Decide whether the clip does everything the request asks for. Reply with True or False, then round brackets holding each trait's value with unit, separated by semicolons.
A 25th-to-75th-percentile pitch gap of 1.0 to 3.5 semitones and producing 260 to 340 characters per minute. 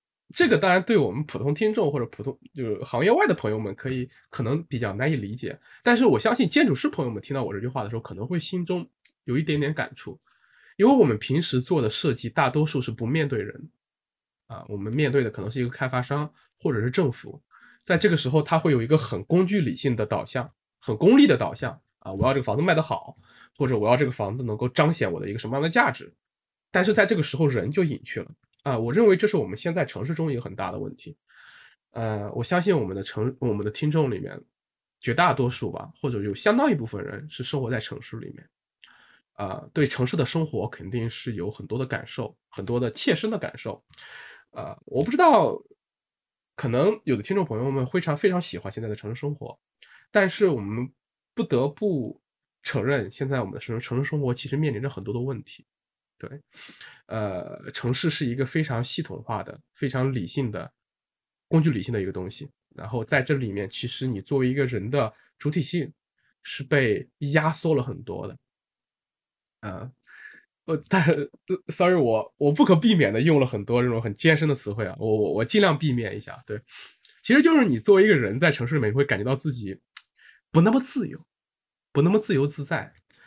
False (5.2 semitones; 315 characters per minute)